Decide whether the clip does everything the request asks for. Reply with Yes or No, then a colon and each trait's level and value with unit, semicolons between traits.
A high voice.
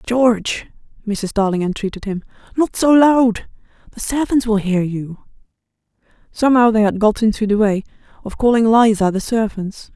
Yes: high, 220 Hz